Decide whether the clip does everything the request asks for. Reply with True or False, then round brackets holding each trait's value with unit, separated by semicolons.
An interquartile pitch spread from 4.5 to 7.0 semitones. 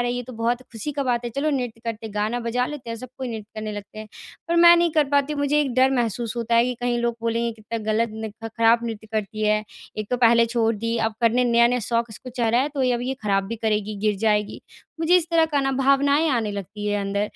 False (2.8 semitones)